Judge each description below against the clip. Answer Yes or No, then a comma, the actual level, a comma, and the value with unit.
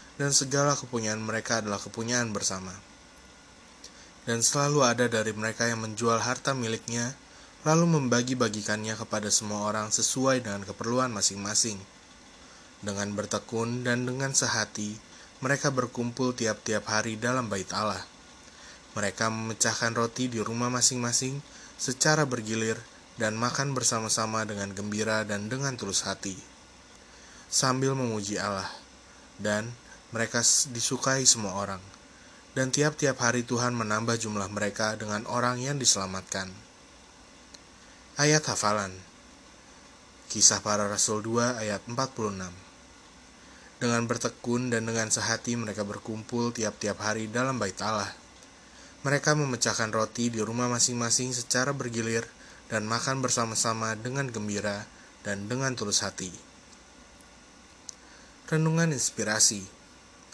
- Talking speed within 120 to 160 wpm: No, average, 110 wpm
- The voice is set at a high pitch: No, low, 115 Hz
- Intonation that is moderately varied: Yes, average, 3.0 semitones